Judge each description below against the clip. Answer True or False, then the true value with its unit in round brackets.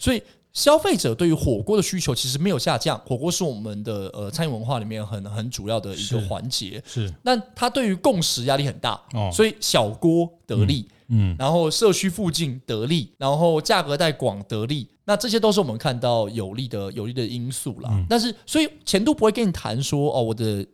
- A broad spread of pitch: True (8.1 semitones)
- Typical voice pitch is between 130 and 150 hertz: True (135 Hz)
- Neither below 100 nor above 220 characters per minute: False (310 characters per minute)